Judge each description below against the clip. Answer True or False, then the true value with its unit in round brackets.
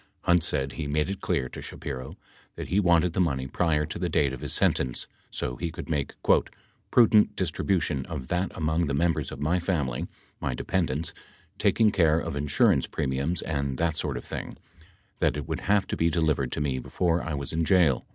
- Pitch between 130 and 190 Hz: False (80 Hz)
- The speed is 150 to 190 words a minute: False (200 wpm)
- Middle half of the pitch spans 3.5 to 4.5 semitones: True (3.8 semitones)